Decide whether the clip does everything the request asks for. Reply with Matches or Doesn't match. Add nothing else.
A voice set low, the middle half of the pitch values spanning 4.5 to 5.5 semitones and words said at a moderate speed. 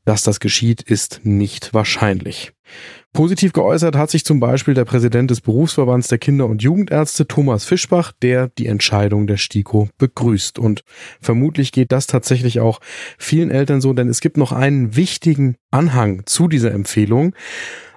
Matches